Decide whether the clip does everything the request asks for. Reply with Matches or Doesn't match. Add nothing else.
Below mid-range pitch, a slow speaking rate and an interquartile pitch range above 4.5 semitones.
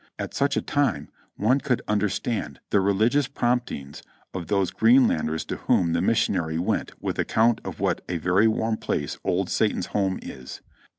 Doesn't match